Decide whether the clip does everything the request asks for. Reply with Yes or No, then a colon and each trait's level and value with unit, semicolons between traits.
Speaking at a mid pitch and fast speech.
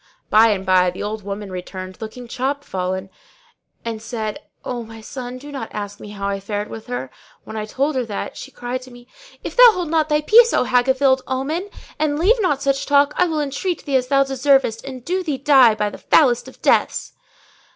No: very high, 255 Hz; fast, 215 wpm